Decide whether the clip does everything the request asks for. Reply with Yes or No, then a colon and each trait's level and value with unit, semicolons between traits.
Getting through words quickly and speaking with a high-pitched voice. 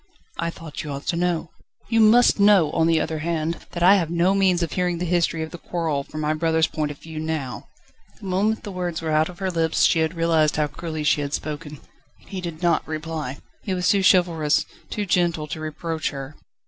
No: fast, 225 wpm; medium, 165 Hz